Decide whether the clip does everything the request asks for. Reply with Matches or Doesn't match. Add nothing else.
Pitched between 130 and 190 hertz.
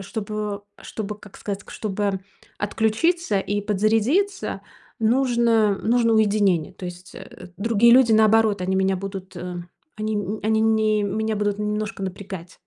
Doesn't match